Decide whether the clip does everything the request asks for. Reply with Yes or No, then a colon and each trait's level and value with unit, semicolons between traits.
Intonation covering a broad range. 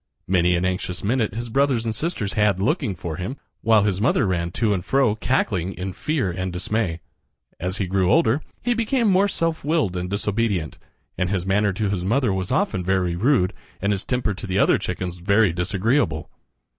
No: average, 4.3 semitones